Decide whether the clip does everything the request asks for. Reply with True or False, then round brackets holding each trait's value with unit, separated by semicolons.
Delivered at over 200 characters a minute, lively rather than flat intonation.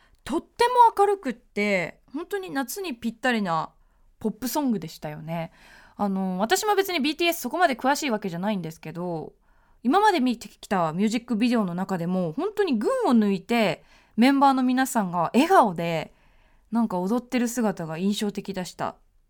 True (355 characters per minute; 6.9 semitones)